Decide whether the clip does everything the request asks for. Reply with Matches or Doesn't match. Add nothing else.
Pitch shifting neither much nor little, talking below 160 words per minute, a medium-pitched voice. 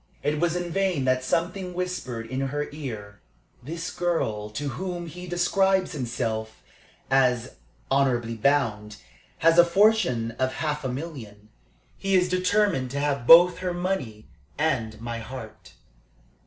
Doesn't match